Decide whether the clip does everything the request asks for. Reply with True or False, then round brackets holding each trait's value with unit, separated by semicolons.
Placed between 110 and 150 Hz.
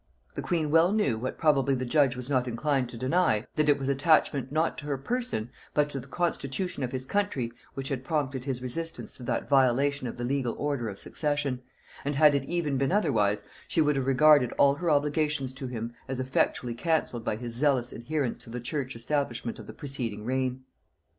True (135 Hz)